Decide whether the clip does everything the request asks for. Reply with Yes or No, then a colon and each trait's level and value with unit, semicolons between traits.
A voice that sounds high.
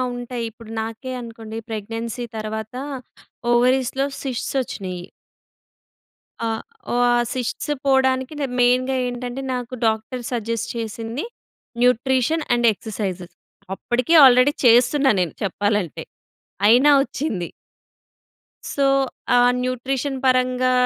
Yes: high, 245 Hz